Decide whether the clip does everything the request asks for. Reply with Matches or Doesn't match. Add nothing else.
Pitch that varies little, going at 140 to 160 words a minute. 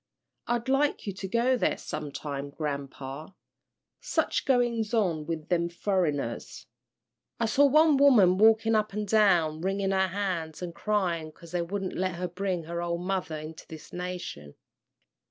Doesn't match